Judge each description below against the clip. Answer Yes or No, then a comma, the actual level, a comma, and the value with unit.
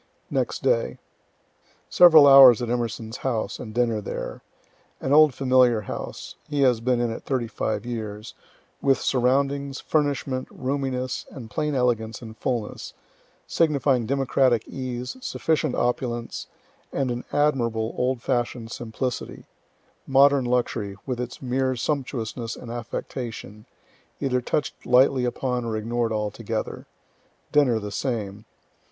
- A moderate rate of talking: No, slow, 125 wpm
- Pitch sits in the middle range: No, low, 125 Hz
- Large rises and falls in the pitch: No, average, 2.8 semitones